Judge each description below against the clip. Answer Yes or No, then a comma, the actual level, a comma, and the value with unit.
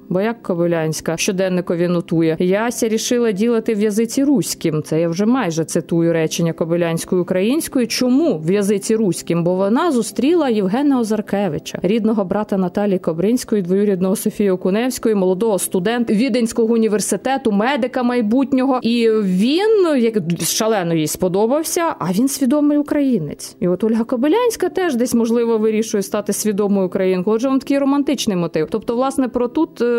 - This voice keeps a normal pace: Yes, average, 140 wpm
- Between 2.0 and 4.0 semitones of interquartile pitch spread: No, average, 4.9 semitones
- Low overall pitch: No, high, 220 Hz